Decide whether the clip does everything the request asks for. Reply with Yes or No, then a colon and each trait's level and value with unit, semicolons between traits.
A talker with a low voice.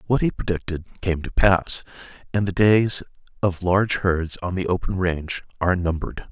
Yes: very low, 90 Hz